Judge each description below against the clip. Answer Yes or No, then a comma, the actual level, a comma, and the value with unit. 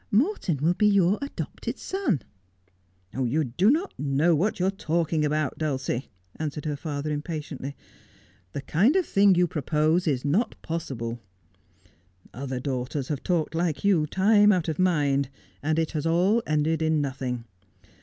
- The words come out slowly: No, average, 155 wpm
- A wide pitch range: No, average, 4.4 semitones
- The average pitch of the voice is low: No, medium, 155 Hz